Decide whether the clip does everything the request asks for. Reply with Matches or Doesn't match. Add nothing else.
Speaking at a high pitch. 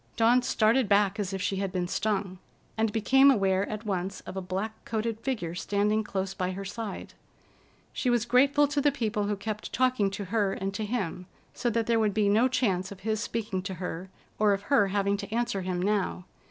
Matches